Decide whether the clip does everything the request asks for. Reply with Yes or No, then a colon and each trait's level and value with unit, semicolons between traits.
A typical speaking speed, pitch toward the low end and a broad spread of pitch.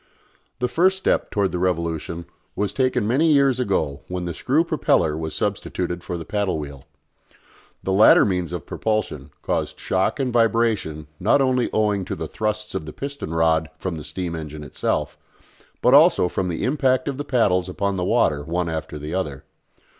Yes: average, 180 wpm; very low, 95 Hz; wide, 7.0 semitones